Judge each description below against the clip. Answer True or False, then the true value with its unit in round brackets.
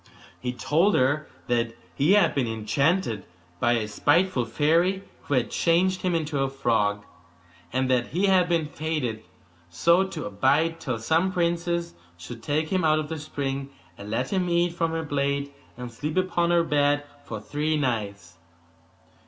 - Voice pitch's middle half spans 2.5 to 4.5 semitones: False (5.6 semitones)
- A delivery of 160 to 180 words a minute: True (165 wpm)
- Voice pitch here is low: False (145 Hz)